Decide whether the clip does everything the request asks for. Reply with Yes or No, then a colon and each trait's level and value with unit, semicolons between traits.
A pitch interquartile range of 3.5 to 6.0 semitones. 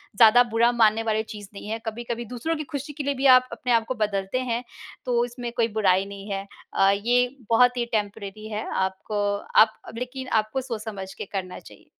No: average, 3.1 semitones